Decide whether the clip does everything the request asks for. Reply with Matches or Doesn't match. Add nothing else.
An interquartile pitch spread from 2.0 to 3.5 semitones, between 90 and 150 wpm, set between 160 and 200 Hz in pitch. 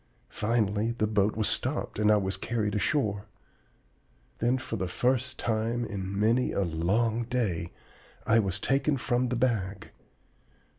Doesn't match